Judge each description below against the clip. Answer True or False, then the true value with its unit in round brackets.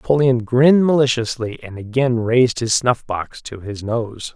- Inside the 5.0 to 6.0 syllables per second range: False (4.6 syllables/s)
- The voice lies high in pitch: False (120 Hz)